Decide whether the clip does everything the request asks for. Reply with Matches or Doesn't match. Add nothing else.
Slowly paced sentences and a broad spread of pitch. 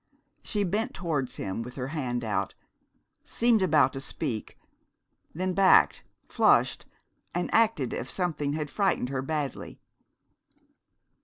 Matches